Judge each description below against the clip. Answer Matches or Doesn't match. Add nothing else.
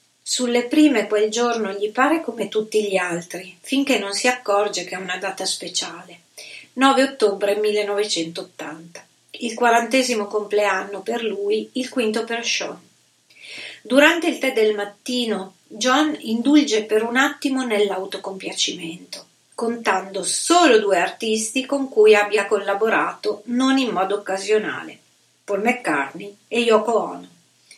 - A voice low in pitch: Doesn't match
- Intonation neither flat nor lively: Matches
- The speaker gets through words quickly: Doesn't match